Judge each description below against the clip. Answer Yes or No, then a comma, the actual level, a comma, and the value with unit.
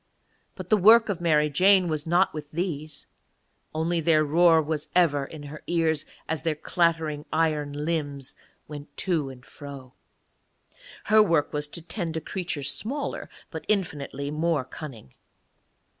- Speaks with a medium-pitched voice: Yes, medium, 155 Hz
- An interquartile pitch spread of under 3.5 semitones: Yes, average, 2.8 semitones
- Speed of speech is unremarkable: Yes, average, 145 wpm